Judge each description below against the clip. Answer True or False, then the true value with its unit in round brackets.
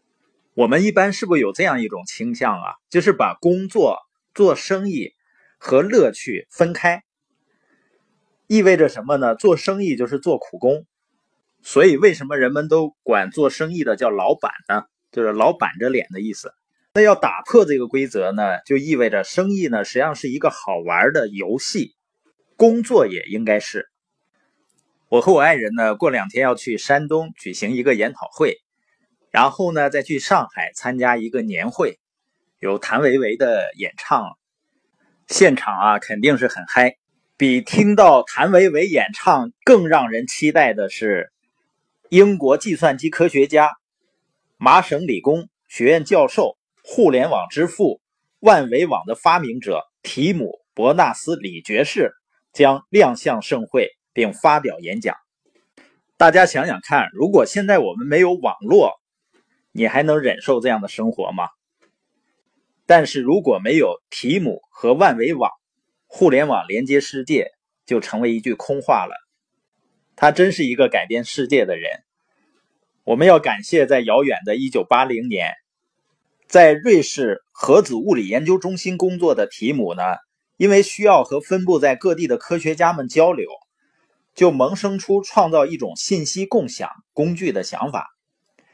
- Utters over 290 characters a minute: False (225 characters per minute)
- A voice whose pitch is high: False (180 Hz)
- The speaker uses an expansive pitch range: True (6.5 semitones)